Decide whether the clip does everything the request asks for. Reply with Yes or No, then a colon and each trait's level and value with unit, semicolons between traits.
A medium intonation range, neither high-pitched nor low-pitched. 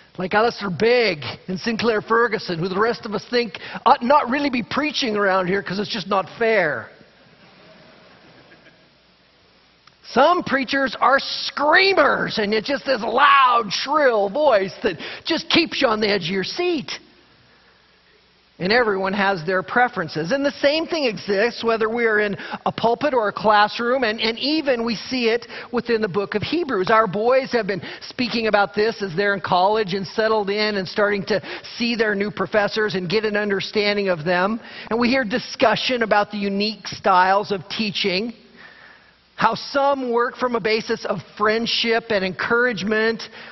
No: average, 3.5 semitones; high, 220 Hz